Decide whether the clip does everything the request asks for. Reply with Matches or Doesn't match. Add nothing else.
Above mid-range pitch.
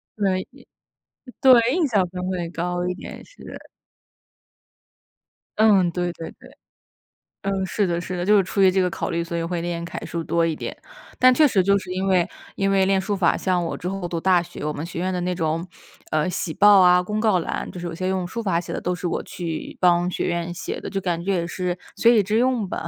Doesn't match